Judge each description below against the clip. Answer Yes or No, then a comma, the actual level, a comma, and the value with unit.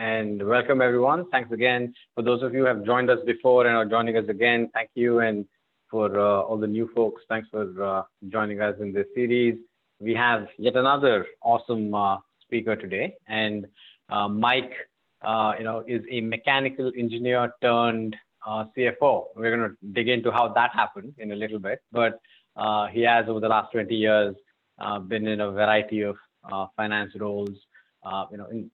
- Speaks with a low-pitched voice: Yes, low, 110 Hz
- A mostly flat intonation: Yes, narrow, 2.3 semitones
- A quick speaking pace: No, average, 190 wpm